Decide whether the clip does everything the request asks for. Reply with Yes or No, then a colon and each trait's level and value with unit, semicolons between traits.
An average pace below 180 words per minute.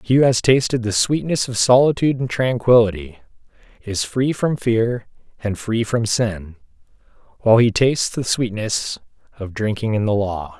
Yes: average, 160 wpm